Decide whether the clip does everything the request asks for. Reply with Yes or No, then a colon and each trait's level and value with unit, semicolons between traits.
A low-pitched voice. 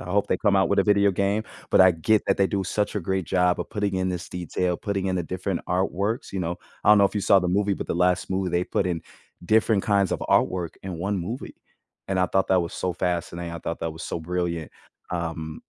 Yes: very low, 95 Hz